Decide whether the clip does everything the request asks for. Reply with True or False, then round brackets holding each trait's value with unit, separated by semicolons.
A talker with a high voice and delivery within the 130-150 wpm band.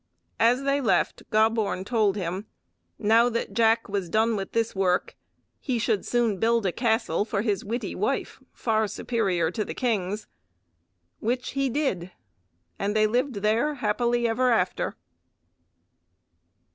True (220 Hz; 140 wpm)